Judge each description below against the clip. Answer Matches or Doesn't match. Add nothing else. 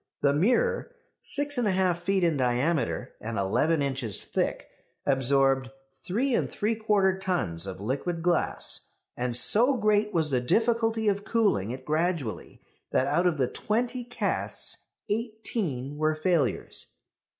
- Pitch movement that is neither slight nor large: Doesn't match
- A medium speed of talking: Doesn't match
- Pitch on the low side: Doesn't match